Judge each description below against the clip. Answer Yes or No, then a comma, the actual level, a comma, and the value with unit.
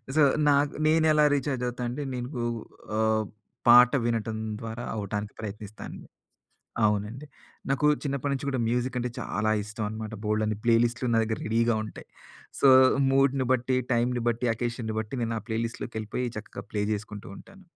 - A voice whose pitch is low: Yes, low, 120 Hz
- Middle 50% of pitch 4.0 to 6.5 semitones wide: No, average, 3.0 semitones